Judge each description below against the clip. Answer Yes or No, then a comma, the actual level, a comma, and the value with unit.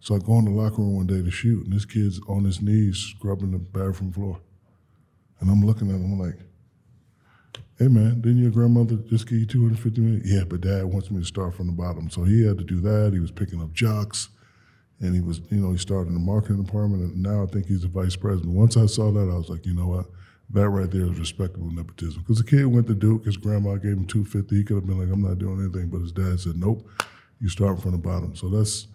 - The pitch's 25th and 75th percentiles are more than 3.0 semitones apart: No, average, 2.7 semitones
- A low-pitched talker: Yes, low, 100 Hz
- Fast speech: Yes, fast, 265 wpm